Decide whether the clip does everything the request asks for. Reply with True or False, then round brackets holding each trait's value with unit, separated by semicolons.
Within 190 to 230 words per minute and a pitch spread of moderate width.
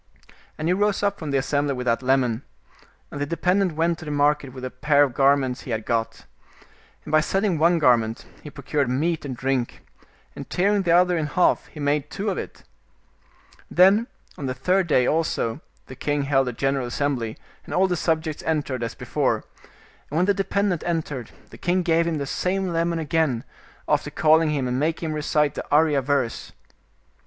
True (200 wpm; 4.2 semitones)